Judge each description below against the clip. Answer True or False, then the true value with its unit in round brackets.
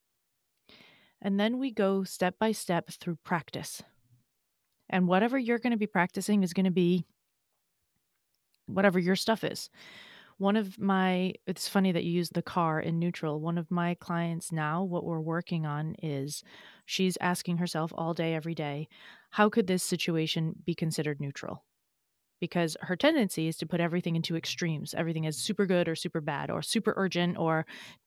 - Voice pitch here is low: False (175 Hz)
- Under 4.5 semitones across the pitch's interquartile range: True (2.7 semitones)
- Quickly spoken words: False (170 wpm)